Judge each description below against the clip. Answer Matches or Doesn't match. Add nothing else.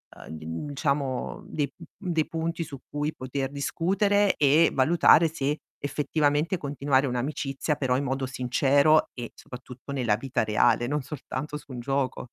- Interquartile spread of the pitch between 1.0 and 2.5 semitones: Doesn't match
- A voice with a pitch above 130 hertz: Matches